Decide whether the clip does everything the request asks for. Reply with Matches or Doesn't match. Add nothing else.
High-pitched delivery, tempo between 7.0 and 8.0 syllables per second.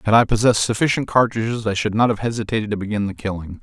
Doesn't match